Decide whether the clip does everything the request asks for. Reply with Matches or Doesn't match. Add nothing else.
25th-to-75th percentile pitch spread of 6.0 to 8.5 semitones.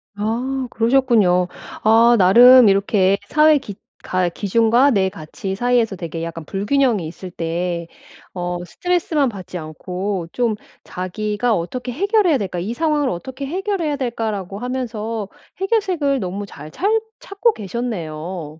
Matches